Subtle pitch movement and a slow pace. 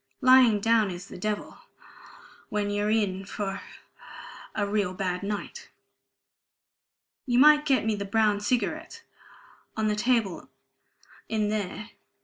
Yes: narrow, 2.3 semitones; slow, 125 wpm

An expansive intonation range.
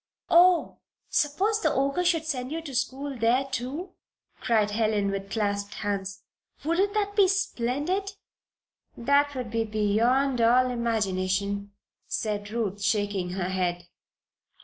Yes: wide, 6.0 semitones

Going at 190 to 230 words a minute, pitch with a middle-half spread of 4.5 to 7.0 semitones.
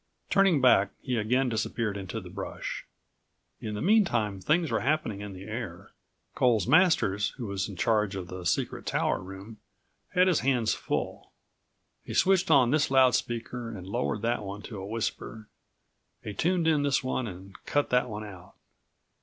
No: average, 170 wpm; average, 5.1 semitones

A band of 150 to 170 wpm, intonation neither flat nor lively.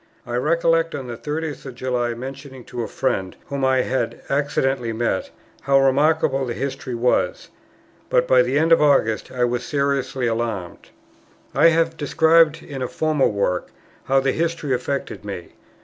Yes: average, 165 wpm; average, 3.9 semitones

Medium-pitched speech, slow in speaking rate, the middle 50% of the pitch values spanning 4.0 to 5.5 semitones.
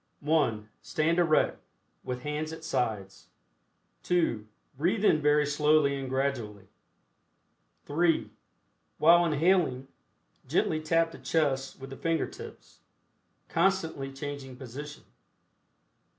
No: medium, 150 Hz; slow, 105 wpm; average, 3.6 semitones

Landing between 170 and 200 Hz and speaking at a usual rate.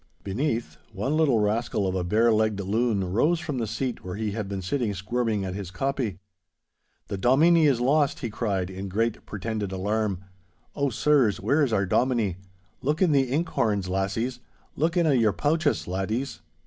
No: low, 110 Hz; average, 180 wpm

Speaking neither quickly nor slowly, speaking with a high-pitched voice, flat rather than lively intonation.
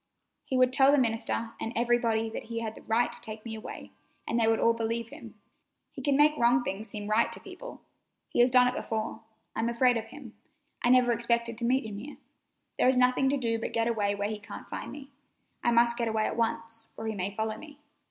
No: fast, 235 wpm; high, 230 Hz; narrow, 2.0 semitones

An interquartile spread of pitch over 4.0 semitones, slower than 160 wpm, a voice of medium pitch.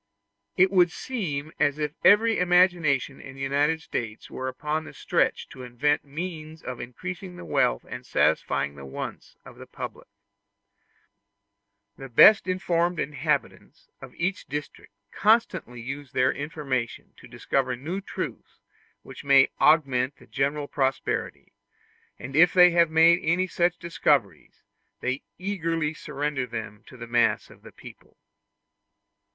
Yes: average, 4.7 semitones; average, 140 wpm; medium, 150 Hz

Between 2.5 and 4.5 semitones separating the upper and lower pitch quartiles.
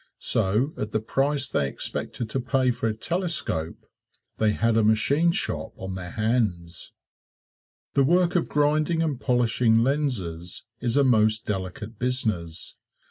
No: average, 5.0 semitones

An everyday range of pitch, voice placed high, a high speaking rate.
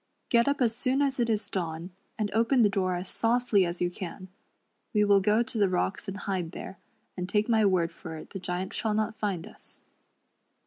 Yes: average, 3.7 semitones; high, 200 Hz; fast, 215 wpm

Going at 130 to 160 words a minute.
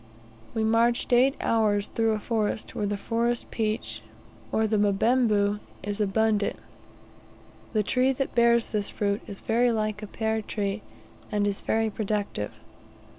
Yes: average, 145 wpm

